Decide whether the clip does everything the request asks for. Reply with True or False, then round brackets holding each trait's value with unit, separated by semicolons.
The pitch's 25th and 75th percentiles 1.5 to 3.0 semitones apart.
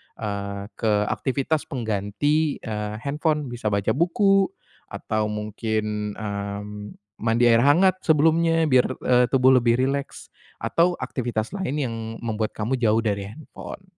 False (5.6 semitones)